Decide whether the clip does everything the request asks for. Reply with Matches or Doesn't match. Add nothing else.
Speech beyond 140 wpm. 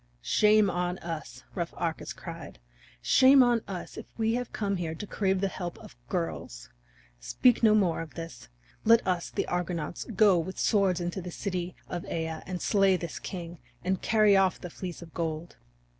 Matches